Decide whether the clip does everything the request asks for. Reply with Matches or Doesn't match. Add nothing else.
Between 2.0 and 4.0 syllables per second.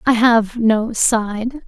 Matches